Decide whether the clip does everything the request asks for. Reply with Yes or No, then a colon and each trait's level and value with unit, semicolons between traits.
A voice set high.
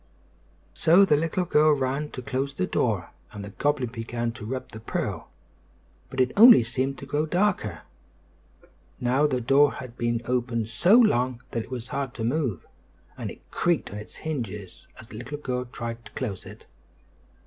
No: low, 130 Hz